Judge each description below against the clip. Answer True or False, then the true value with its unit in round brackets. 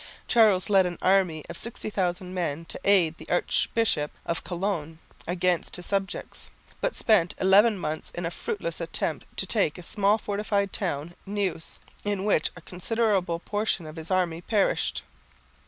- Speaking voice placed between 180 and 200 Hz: True (185 Hz)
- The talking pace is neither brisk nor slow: True (155 wpm)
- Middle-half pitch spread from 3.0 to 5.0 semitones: True (3.3 semitones)